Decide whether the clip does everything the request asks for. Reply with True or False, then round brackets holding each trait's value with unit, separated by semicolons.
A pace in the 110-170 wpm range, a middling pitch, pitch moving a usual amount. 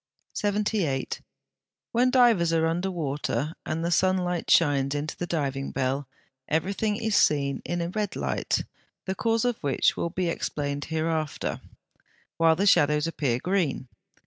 True (145 wpm; 165 Hz; 4.8 semitones)